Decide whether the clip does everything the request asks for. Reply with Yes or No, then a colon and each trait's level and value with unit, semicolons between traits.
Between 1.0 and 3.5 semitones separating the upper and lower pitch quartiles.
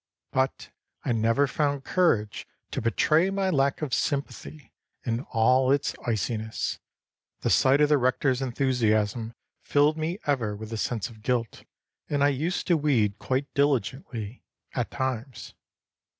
No: average, 3.9 semitones